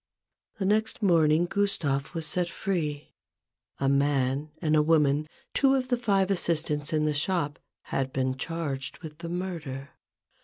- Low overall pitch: No, medium, 155 Hz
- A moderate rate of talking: Yes, average, 150 wpm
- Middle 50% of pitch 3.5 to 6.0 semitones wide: Yes, average, 4.1 semitones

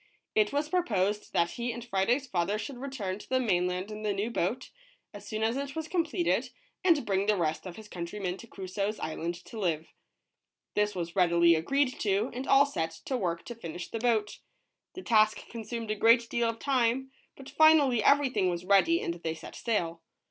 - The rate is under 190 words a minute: No, average, 200 wpm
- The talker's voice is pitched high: Yes, high, 215 Hz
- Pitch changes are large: Yes, wide, 5.7 semitones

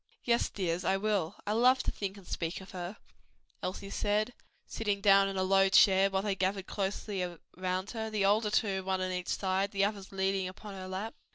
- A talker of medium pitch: No, high, 195 Hz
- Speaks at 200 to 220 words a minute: Yes, fast, 205 wpm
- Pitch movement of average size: No, narrow, 1.7 semitones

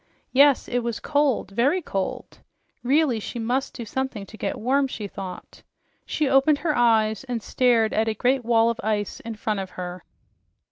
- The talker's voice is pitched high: Yes, high, 235 Hz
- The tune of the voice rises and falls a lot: No, average, 3.8 semitones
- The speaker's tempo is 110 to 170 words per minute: No, average, 180 wpm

